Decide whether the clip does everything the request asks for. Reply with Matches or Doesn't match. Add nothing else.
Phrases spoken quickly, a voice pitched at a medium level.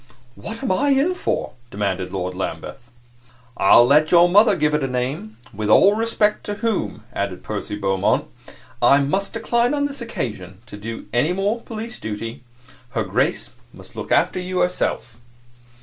Doesn't match